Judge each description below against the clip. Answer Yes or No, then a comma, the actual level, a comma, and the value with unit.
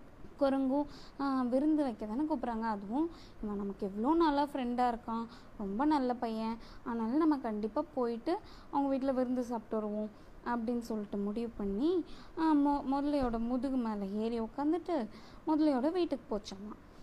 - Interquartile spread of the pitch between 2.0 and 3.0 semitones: No, average, 4.5 semitones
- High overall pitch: Yes, very high, 255 Hz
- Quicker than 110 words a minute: Yes, average, 125 wpm